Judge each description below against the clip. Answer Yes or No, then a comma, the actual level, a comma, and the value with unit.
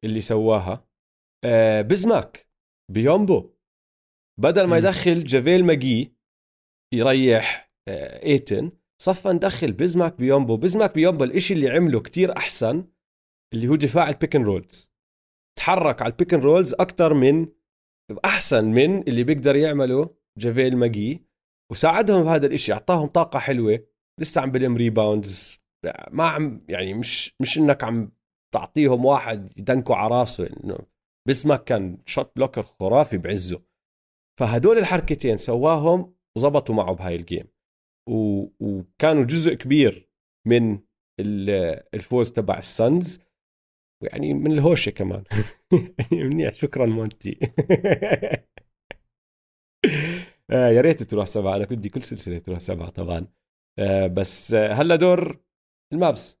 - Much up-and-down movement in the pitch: Yes, wide, 7.6 semitones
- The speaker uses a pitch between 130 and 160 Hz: No, low, 120 Hz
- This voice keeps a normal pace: Yes, average, 110 wpm